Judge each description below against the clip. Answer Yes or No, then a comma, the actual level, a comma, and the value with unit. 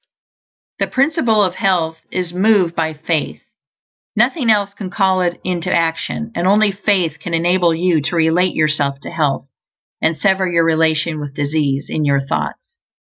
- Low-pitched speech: No, medium, 170 Hz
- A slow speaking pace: No, average, 160 wpm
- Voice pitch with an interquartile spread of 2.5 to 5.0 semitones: Yes, average, 3.4 semitones